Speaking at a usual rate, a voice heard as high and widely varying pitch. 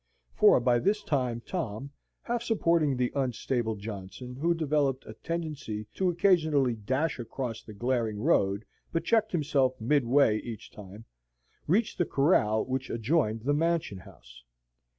No: average, 145 wpm; low, 130 Hz; wide, 6.3 semitones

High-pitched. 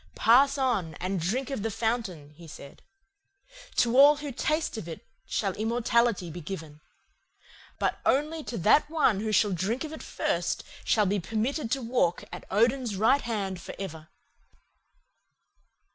Yes: high, 220 Hz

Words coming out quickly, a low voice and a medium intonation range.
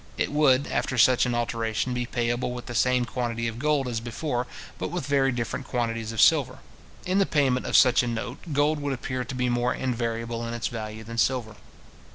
No: fast, 210 wpm; low, 125 Hz; narrow, 2.2 semitones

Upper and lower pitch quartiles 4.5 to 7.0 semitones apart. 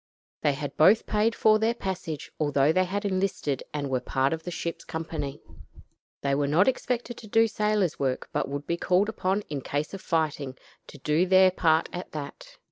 Yes: wide, 5.4 semitones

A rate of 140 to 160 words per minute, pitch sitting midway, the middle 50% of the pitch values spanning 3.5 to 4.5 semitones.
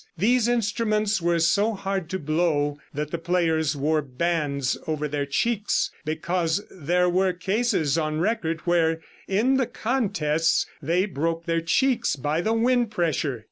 No: average, 145 wpm; medium, 170 Hz; average, 4.9 semitones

